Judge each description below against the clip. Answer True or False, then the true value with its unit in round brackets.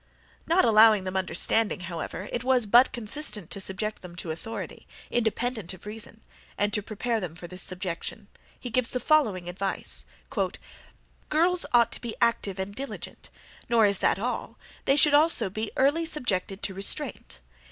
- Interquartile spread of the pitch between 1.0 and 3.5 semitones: False (4.5 semitones)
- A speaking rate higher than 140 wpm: True (165 wpm)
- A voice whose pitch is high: True (215 Hz)